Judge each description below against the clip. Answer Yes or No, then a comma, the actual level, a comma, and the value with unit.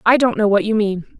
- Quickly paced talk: Yes, fast, 300 wpm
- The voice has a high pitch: Yes, high, 215 Hz